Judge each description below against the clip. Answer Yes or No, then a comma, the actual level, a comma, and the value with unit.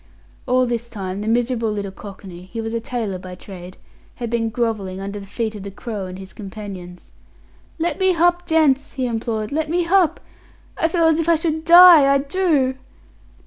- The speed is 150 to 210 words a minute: Yes, average, 190 wpm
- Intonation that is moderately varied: No, wide, 7.9 semitones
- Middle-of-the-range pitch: No, high, 235 Hz